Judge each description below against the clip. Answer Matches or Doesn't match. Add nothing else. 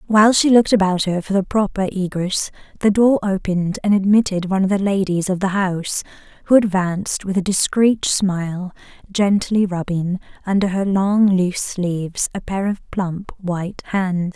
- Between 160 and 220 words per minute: Matches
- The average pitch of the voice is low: Doesn't match